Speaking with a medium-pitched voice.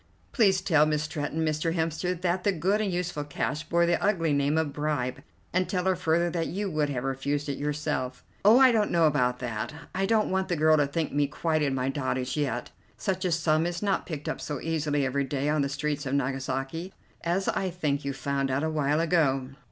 Yes: medium, 155 Hz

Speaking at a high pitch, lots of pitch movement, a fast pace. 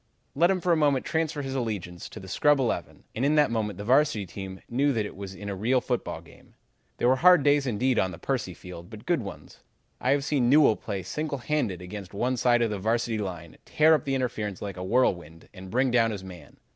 No: low, 115 Hz; wide, 6.1 semitones; fast, 235 wpm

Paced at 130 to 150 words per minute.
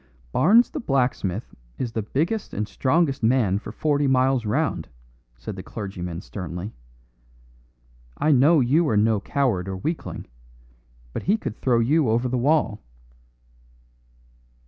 Yes: slow, 135 wpm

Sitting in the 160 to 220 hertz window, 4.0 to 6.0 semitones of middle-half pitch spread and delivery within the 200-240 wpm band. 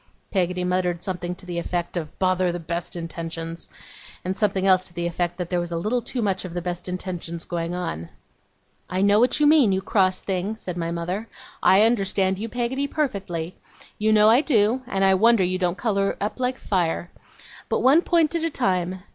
No: medium, 185 Hz; average, 3.6 semitones; fast, 205 wpm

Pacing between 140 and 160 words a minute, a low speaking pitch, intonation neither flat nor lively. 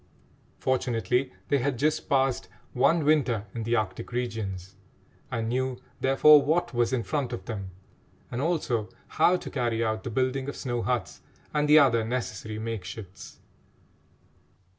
Yes: average, 145 wpm; low, 125 Hz; average, 3.5 semitones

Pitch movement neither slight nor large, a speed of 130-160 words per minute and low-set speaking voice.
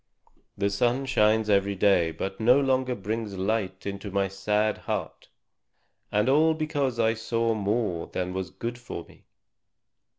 Yes: average, 3.6 semitones; average, 145 wpm; low, 105 Hz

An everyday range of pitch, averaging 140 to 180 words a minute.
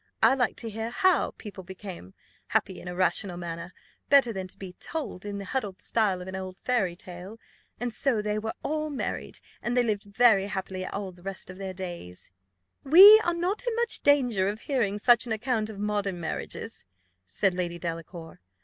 No: average, 4.8 semitones; average, 195 wpm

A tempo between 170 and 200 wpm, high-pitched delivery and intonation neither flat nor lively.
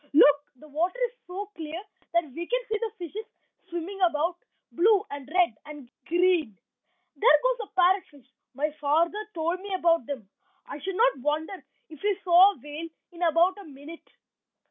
Yes: average, 175 wpm; very high, 340 Hz; average, 4.2 semitones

